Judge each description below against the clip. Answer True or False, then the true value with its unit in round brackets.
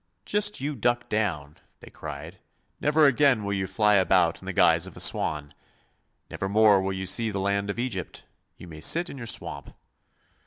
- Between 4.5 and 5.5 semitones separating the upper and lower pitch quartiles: True (4.8 semitones)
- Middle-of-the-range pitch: False (105 Hz)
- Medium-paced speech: True (190 wpm)